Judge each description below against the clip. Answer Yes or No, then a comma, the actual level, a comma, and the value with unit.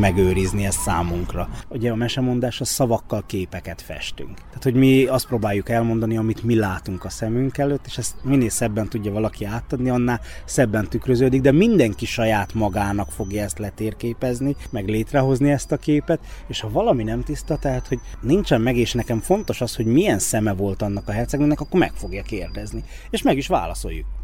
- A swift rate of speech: Yes, fast, 180 wpm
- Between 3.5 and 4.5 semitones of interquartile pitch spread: Yes, average, 4.0 semitones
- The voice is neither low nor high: No, low, 115 Hz